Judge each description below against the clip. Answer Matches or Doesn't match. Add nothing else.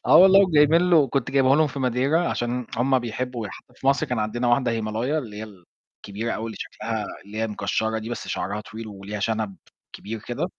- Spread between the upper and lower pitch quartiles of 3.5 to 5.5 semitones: Matches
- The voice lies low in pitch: Matches